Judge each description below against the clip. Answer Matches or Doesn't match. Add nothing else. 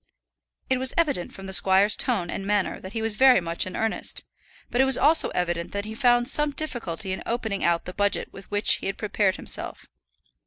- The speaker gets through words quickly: Matches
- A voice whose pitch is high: Matches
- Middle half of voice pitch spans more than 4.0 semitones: Matches